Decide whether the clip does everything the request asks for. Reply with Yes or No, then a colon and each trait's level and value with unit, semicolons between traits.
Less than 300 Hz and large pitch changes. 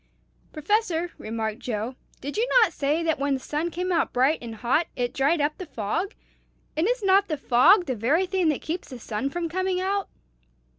No: very high, 315 Hz; wide, 6.0 semitones